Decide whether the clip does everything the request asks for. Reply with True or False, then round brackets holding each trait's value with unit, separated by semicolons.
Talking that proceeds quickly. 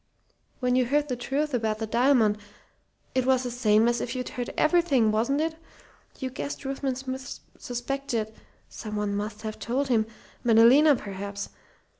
False (155 wpm)